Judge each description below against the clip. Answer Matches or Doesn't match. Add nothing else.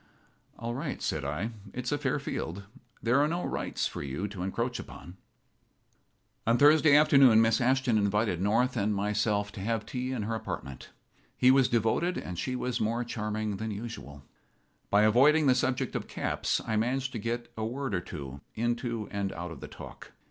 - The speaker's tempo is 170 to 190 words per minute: Matches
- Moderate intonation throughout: Matches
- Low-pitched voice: Matches